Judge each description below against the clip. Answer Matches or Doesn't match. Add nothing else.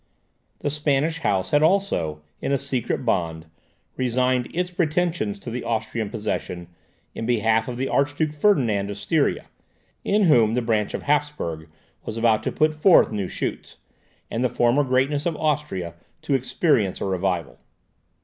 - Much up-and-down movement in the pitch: Matches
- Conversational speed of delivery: Matches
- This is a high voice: Doesn't match